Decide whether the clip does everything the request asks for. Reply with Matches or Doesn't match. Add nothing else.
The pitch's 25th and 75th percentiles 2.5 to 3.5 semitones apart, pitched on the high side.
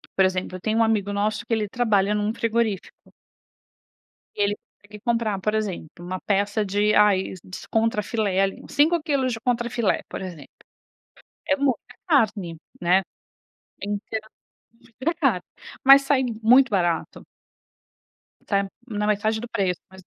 Matches